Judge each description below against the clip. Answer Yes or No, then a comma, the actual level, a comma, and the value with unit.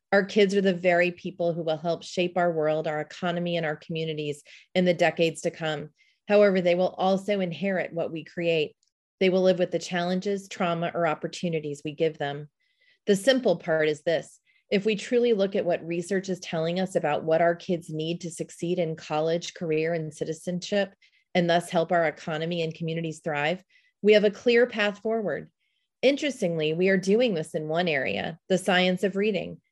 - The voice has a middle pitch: Yes, medium, 175 Hz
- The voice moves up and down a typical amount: Yes, average, 3.3 semitones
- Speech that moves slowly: No, average, 190 wpm